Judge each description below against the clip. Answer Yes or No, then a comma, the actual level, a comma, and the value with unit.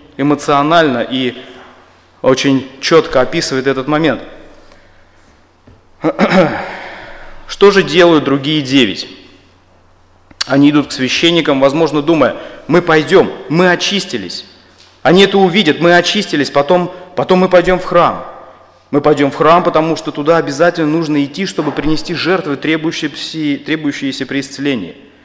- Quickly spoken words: No, average, 115 wpm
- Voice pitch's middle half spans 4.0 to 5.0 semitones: Yes, average, 4.4 semitones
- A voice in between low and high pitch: Yes, medium, 150 Hz